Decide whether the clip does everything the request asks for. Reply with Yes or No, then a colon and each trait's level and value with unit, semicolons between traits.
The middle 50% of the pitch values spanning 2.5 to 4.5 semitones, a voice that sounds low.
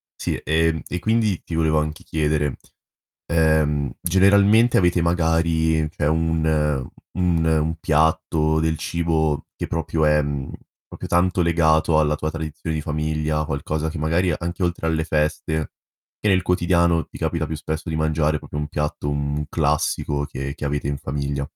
No: narrow, 1.7 semitones; very low, 80 Hz